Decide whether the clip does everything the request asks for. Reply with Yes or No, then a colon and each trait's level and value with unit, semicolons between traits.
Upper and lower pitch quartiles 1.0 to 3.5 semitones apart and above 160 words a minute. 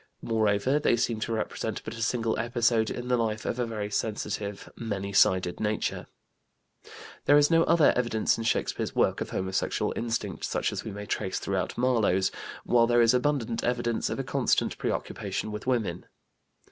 Yes: average, 2.8 semitones; average, 170 wpm